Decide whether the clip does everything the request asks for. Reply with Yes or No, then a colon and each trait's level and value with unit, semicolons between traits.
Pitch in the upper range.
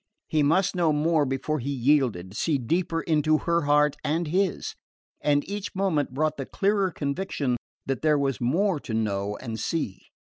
No: medium, 150 Hz